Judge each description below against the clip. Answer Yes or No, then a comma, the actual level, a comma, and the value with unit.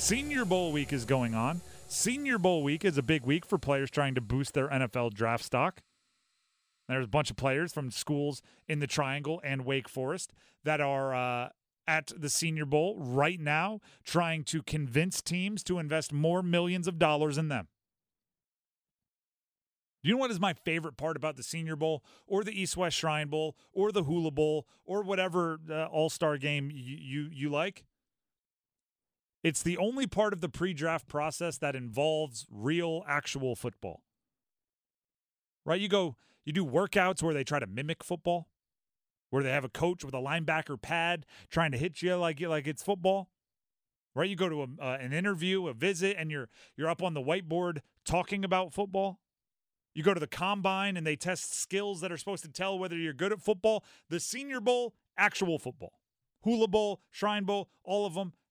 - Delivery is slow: No, average, 185 wpm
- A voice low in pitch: No, medium, 160 Hz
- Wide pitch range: No, average, 4.5 semitones